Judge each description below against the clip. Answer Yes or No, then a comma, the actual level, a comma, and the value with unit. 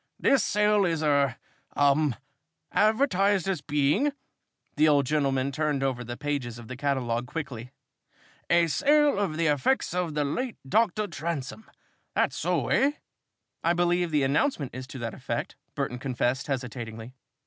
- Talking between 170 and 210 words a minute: No, average, 150 wpm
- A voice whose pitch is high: No, medium, 150 Hz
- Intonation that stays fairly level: No, wide, 5.6 semitones